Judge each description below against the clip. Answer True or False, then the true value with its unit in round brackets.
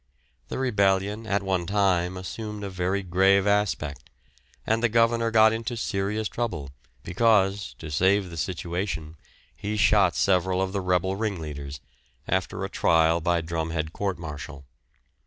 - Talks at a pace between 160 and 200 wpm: False (140 wpm)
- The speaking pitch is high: False (95 Hz)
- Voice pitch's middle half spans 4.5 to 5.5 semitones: False (3.5 semitones)